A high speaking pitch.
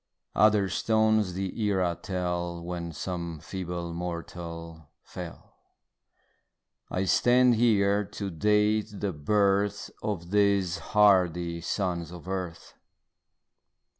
No: very low, 95 Hz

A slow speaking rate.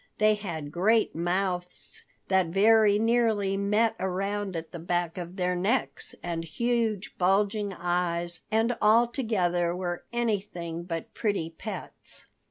Yes: slow, 125 wpm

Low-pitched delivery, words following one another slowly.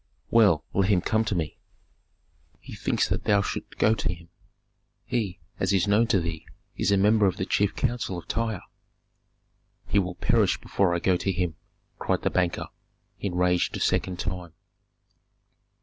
No: very low, 95 Hz; average, 165 wpm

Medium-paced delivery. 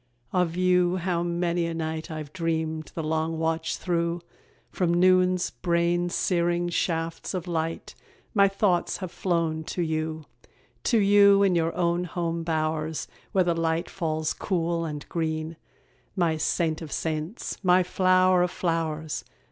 Yes: average, 145 wpm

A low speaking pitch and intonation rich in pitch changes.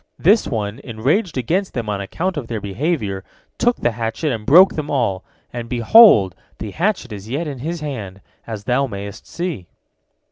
Yes: low, 120 Hz; wide, 7.6 semitones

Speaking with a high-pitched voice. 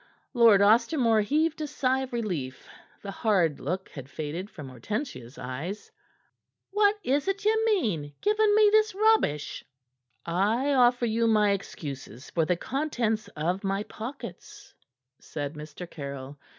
Yes: high, 215 Hz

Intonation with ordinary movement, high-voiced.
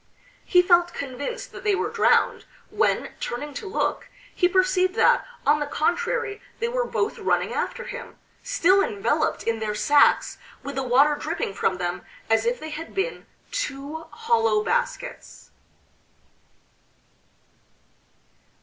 No: wide, 7.2 semitones; very high, 330 Hz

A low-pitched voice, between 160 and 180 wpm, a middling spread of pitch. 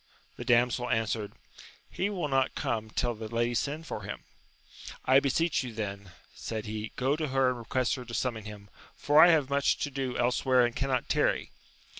No: low, 125 Hz; average, 190 wpm; average, 3.4 semitones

